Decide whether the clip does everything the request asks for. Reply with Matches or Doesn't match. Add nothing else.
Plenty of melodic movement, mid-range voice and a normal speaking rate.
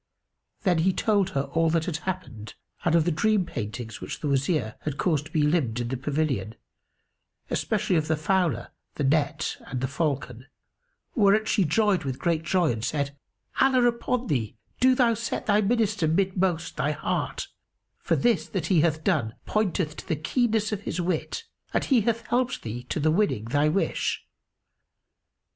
Matches